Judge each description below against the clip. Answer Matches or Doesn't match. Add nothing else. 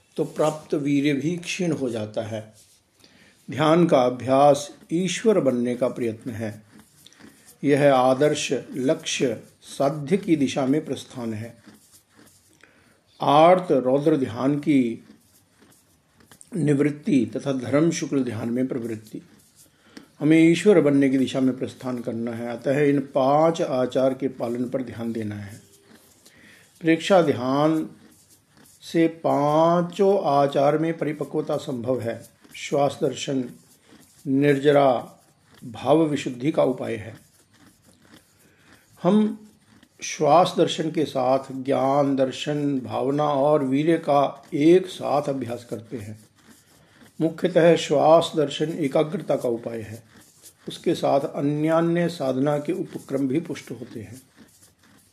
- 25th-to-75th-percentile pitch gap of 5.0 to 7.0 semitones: Doesn't match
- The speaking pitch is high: Doesn't match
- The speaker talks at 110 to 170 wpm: Matches